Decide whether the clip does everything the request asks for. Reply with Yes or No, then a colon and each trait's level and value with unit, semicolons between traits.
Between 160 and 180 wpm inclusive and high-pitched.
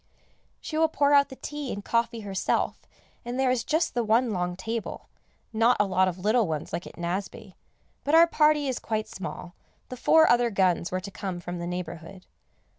No: average, 195 wpm; high, 220 Hz